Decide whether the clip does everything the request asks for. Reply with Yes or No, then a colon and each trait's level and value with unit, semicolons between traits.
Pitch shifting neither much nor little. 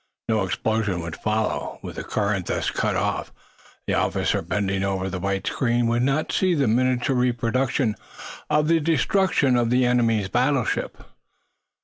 Yes: average, 3.9 semitones